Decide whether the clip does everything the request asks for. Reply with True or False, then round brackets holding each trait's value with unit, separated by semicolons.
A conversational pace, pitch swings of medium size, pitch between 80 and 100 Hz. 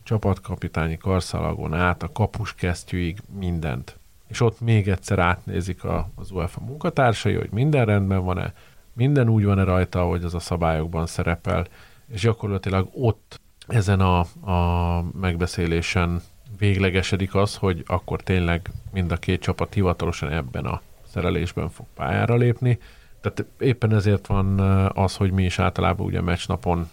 True (140 wpm; 3.3 semitones; 95 Hz)